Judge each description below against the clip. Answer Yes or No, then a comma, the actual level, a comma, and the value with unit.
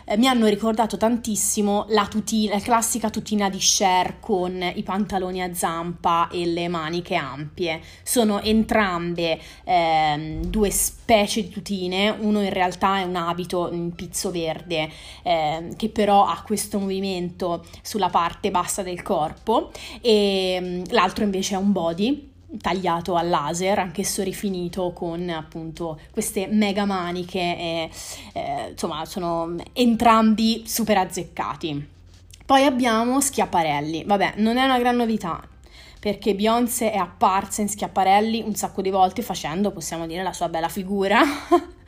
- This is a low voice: No, high, 195 Hz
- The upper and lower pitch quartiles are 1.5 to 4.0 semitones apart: Yes, average, 3.7 semitones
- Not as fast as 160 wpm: Yes, average, 140 wpm